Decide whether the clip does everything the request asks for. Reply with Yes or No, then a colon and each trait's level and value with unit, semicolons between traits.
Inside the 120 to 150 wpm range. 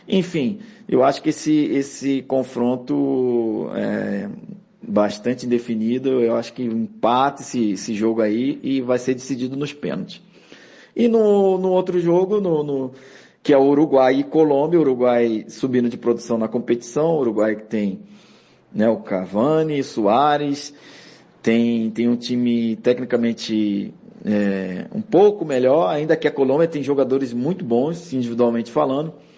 Yes: average, 145 wpm